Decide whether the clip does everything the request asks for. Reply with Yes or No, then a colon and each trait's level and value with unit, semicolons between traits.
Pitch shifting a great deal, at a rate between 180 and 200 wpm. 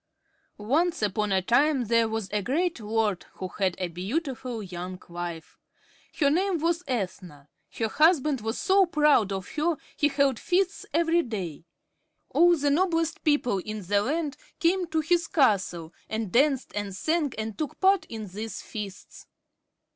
No: wide, 8.0 semitones; average, 155 wpm